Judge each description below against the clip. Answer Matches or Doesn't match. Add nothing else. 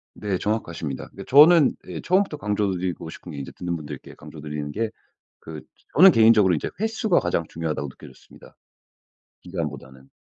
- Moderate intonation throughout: Doesn't match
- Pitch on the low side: Matches